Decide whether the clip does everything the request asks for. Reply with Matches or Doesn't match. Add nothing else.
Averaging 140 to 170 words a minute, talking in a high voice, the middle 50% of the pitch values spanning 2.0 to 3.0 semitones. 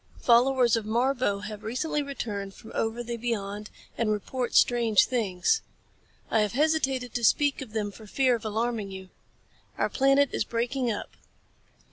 Doesn't match